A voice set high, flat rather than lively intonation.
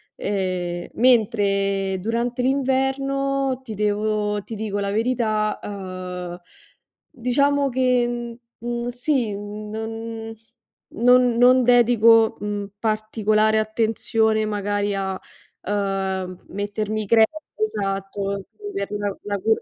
No: high, 215 Hz; average, 3.1 semitones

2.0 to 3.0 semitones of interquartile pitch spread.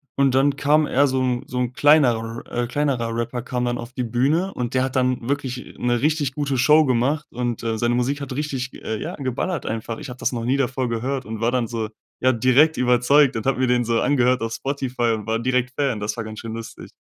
Yes: average, 2.7 semitones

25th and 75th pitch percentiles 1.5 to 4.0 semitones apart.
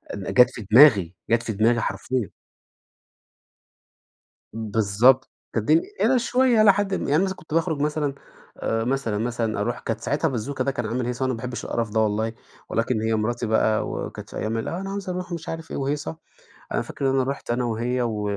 No: average, 5.1 semitones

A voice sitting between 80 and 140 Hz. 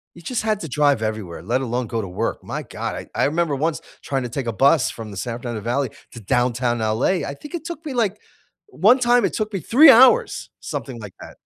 Yes: low, 135 Hz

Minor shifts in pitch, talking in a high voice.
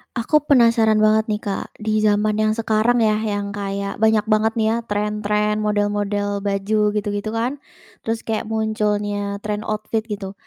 Yes: narrow, 1.2 semitones; high, 215 Hz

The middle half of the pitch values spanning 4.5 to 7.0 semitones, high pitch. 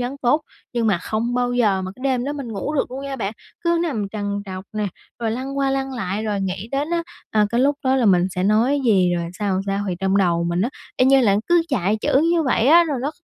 Yes: wide, 5.5 semitones; high, 235 Hz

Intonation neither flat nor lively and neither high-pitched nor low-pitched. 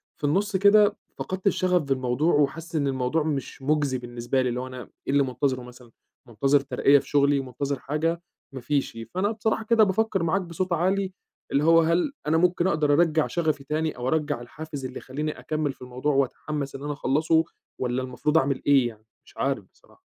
Yes: average, 4.1 semitones; medium, 145 Hz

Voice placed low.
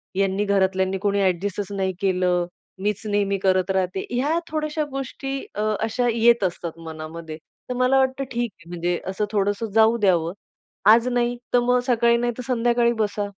No: high, 205 Hz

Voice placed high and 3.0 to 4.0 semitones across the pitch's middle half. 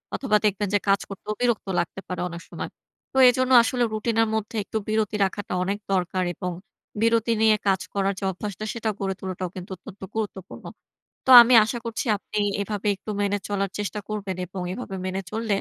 No: high, 205 Hz; narrow, 2.5 semitones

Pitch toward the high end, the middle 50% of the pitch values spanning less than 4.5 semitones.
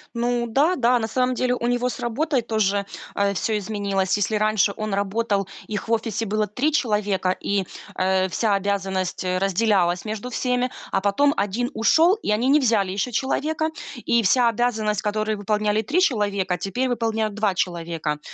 Yes: high, 215 Hz; average, 3.5 semitones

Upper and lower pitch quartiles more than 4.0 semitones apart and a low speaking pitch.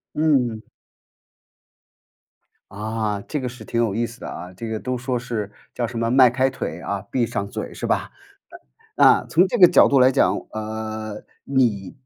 No: average, 3.0 semitones; low, 115 Hz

